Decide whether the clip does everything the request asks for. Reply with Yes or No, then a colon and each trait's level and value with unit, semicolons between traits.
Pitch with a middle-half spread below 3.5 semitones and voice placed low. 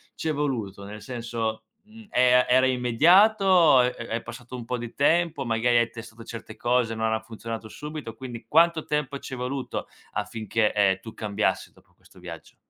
No: average, 4.0 semitones; low, 120 Hz